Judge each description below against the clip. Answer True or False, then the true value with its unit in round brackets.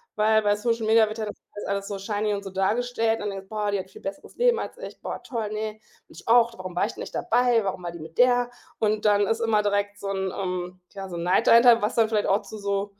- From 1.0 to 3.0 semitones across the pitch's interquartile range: True (2.4 semitones)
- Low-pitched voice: False (210 Hz)